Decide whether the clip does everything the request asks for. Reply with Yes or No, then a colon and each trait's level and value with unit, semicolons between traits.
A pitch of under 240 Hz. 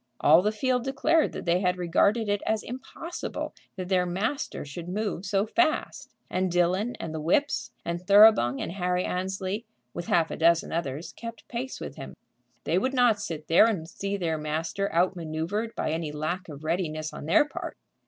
Yes: medium, 185 Hz